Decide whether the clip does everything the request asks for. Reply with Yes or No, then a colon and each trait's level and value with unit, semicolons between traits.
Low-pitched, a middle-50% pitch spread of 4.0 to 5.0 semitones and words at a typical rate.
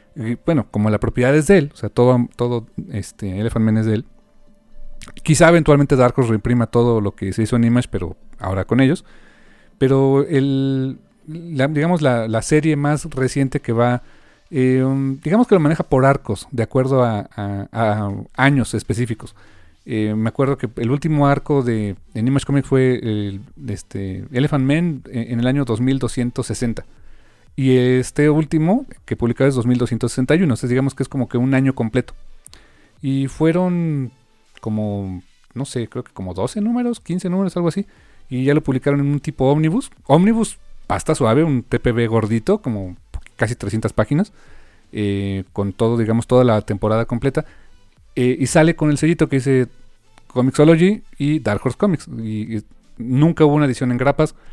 Yes: low, 125 Hz; average, 4.3 semitones; average, 170 wpm